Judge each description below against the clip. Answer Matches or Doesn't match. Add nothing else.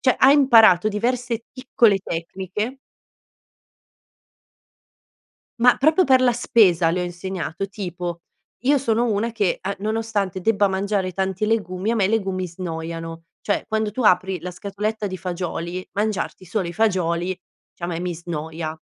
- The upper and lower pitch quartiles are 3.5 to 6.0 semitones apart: Matches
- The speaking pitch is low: Doesn't match